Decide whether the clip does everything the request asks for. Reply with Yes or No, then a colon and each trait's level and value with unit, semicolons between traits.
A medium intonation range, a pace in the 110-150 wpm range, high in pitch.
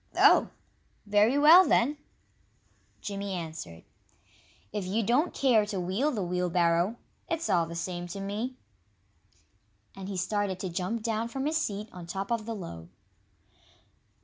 Yes: average, 4.4 semitones; average, 145 wpm; high, 200 Hz